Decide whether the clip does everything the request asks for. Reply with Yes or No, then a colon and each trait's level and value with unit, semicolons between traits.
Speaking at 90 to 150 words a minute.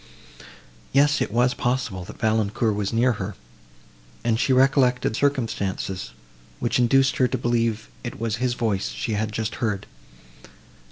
Yes: average, 145 wpm